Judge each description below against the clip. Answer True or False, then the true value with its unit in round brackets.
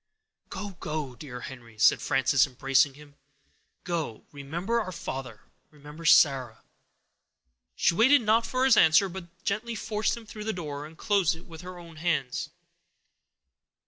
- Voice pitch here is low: False (160 Hz)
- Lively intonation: True (6.2 semitones)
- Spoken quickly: False (145 wpm)